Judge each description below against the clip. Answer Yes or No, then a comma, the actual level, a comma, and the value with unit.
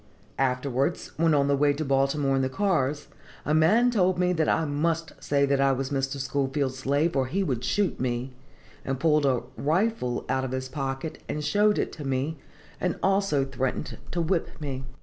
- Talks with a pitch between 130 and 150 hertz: Yes, medium, 140 Hz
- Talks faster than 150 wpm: Yes, average, 190 wpm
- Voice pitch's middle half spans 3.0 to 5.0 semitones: Yes, average, 3.5 semitones